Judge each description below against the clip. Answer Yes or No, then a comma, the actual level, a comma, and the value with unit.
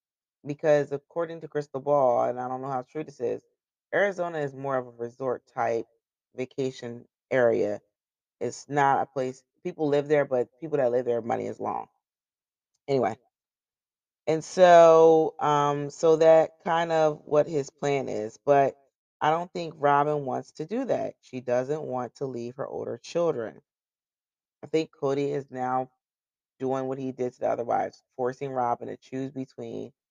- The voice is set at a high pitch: No, medium, 140 Hz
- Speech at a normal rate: Yes, average, 165 wpm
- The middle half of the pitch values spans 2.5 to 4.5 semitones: Yes, average, 3.3 semitones